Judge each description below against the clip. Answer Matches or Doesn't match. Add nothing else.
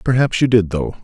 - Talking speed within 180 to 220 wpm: Doesn't match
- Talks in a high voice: Doesn't match